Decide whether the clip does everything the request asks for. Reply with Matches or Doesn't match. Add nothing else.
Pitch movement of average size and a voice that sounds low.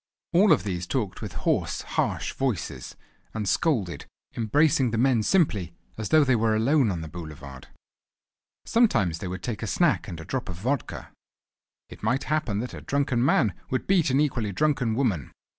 Doesn't match